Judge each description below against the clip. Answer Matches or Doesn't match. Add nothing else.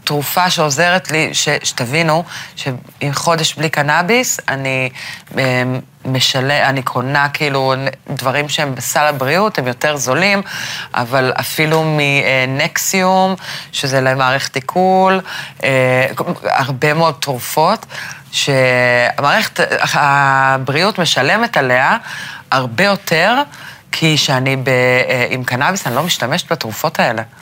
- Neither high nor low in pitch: Matches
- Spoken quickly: Doesn't match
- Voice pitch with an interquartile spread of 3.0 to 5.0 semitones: Matches